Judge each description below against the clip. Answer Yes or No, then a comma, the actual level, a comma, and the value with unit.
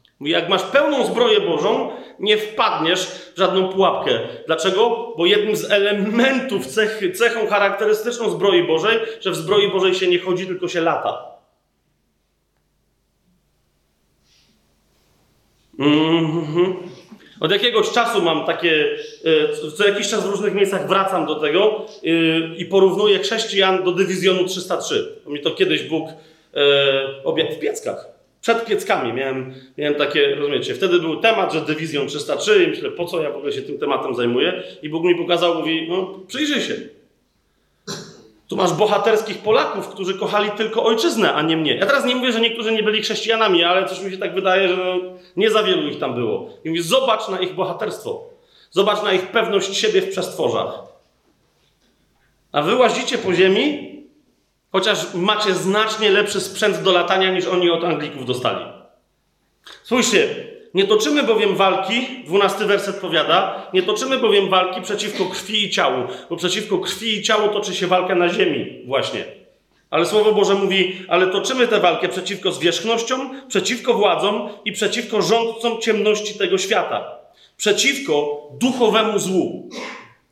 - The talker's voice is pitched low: No, high, 200 Hz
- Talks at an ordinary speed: Yes, average, 150 wpm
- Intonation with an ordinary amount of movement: Yes, average, 4.1 semitones